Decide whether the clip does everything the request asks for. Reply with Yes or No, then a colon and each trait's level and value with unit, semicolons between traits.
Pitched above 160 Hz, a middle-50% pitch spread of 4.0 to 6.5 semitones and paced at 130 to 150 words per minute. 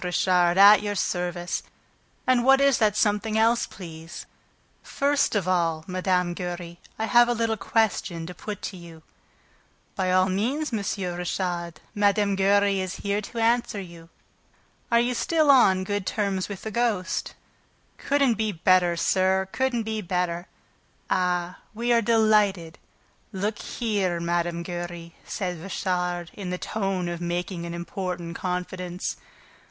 No: high, 190 Hz; average, 3.6 semitones; average, 145 wpm